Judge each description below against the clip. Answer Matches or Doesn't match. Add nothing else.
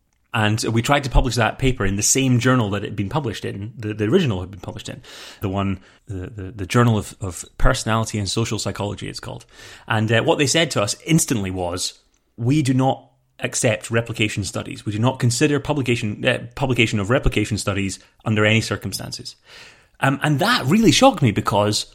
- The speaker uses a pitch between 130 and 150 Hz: Doesn't match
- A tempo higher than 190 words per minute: Matches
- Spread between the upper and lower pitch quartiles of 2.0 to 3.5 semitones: Doesn't match